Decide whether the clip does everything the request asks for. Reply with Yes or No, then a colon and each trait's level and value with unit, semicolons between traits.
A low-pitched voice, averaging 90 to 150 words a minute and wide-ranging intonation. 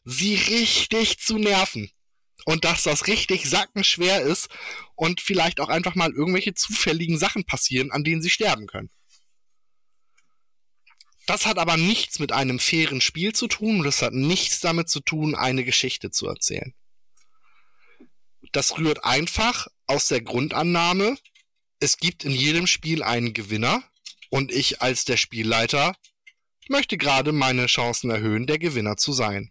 No: medium, 165 Hz; average, 145 wpm; wide, 7.5 semitones